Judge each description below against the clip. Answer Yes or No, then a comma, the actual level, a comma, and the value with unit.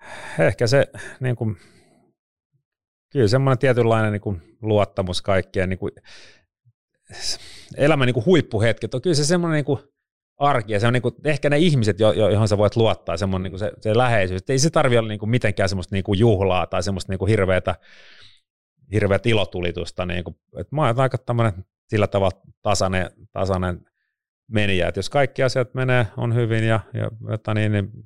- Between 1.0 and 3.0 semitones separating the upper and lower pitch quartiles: No, average, 4.3 semitones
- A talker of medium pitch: No, low, 110 Hz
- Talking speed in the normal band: No, fast, 160 wpm